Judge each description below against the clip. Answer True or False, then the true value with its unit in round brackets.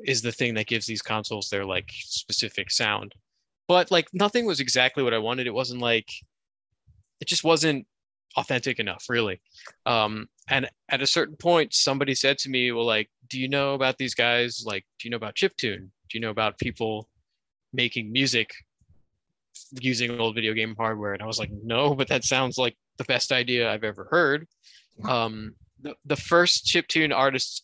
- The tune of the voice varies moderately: True (3.8 semitones)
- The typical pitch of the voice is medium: False (120 Hz)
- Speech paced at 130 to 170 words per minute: False (185 wpm)